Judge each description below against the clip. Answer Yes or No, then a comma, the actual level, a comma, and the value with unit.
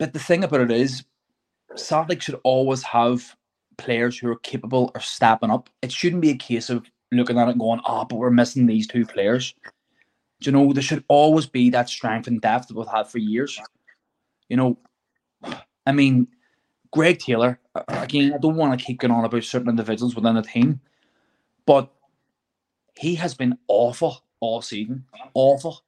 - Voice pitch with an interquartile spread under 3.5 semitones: Yes, average, 2.9 semitones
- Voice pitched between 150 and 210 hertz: No, low, 125 Hz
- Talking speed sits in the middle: Yes, average, 185 wpm